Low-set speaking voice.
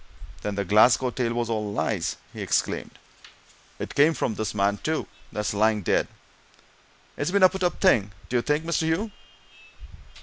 Yes: low, 120 Hz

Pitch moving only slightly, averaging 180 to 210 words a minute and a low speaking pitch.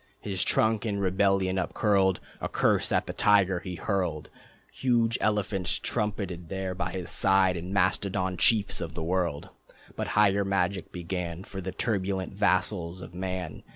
No: narrow, 1.8 semitones; average, 155 wpm; very low, 95 Hz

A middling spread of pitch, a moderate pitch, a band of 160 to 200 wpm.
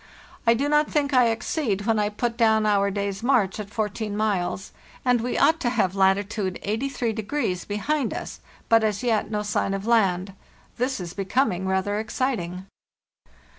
No: average, 3.5 semitones; high, 215 Hz; average, 170 wpm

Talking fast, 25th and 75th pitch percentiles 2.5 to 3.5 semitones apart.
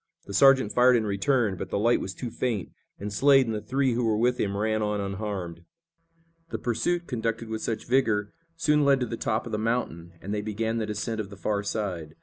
Yes: fast, 225 wpm; average, 3.2 semitones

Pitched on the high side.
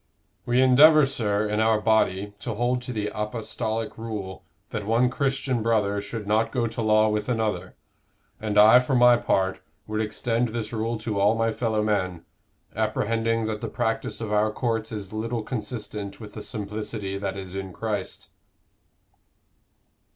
No: low, 110 Hz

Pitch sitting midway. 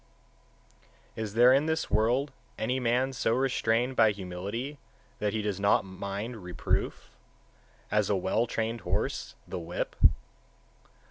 No: low, 110 Hz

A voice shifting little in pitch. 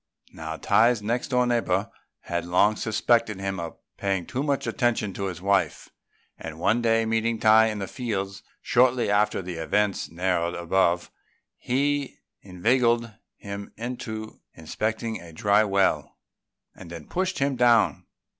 No: average, 4.1 semitones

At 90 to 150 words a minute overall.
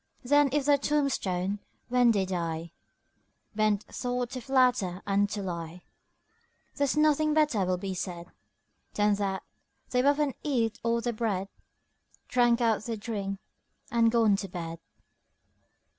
Yes: average, 140 wpm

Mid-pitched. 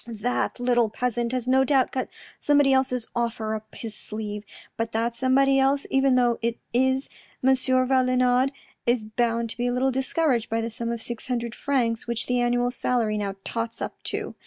No: high, 245 Hz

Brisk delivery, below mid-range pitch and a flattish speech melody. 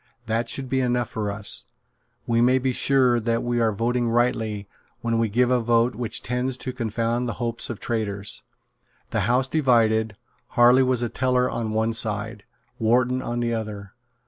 No: average, 175 wpm; low, 120 Hz; narrow, 1.9 semitones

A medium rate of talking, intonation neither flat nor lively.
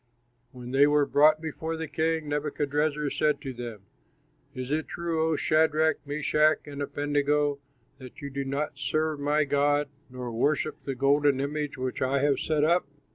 No: average, 165 wpm; narrow, 1.8 semitones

